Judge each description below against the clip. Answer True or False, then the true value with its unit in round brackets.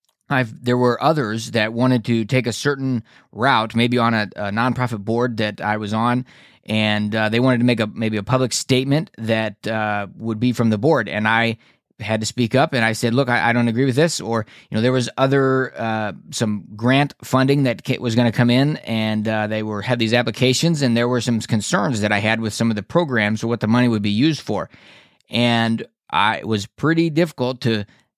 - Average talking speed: False (225 wpm)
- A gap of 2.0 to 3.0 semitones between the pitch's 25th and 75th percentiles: True (2.6 semitones)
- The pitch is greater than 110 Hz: True (120 Hz)